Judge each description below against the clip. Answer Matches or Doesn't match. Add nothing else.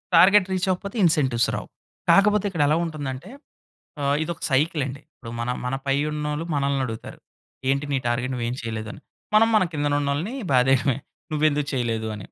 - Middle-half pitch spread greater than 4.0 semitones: Matches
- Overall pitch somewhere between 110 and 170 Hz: Matches